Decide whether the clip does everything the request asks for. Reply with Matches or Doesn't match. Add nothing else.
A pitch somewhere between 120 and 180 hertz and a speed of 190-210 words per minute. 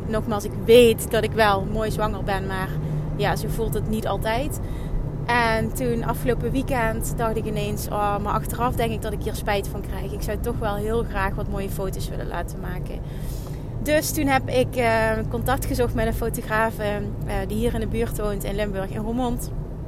Matches